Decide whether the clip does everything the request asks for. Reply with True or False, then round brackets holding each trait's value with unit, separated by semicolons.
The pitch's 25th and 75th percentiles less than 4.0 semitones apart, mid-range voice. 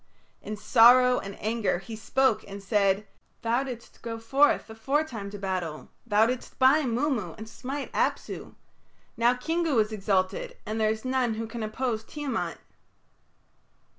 False (3.5 semitones; 225 Hz)